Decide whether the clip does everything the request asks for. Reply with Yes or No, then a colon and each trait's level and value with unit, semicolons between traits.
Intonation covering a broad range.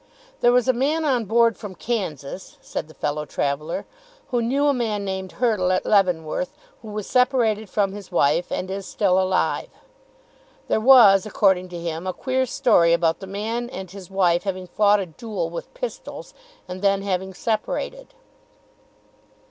No: average, 4.4 semitones